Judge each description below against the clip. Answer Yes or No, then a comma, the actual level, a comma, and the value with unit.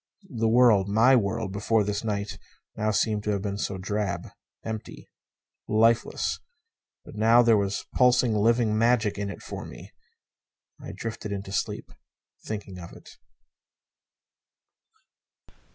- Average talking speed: No, slow, 130 wpm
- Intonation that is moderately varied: No, narrow, 2.2 semitones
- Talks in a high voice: No, low, 105 Hz